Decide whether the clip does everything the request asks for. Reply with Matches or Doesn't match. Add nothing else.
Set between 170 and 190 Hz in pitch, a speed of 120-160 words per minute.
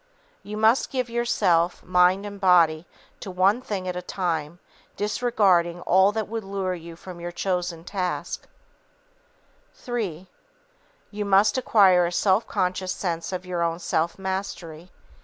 Matches